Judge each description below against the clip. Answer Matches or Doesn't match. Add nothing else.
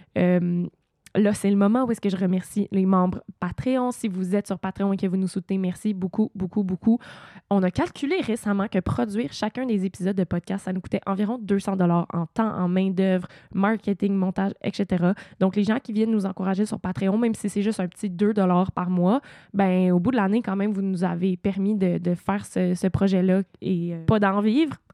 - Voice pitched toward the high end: Matches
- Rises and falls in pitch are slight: Matches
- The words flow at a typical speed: Doesn't match